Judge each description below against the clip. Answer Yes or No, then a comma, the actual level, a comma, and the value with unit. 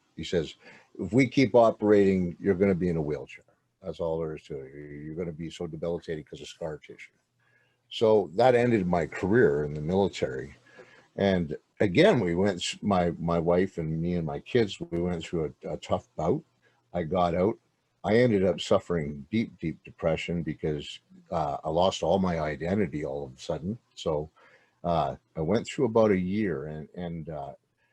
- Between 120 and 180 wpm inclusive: No, average, 190 wpm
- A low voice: Yes, very low, 85 Hz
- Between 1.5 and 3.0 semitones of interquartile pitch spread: No, average, 3.7 semitones